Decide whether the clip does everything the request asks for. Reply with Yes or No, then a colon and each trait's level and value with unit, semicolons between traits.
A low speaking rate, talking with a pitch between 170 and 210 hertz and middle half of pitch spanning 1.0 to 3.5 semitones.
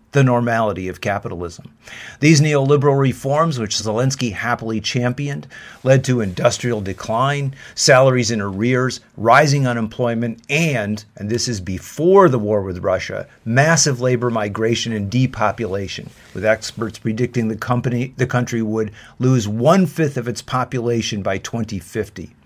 No: slow, 135 wpm; low, 120 Hz; average, 3.0 semitones